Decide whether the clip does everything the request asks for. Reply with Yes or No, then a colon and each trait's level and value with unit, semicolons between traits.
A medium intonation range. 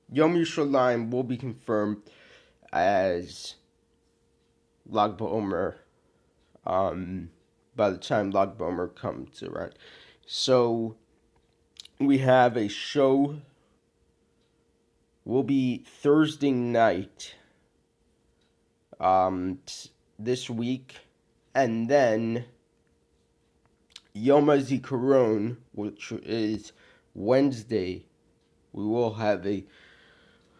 Yes: average, 4.4 semitones